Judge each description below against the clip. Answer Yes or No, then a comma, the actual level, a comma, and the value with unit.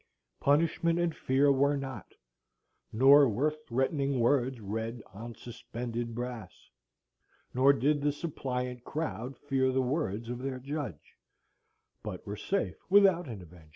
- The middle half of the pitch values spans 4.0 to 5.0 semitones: No, average, 3.5 semitones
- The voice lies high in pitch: No, low, 130 Hz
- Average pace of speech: No, slow, 130 wpm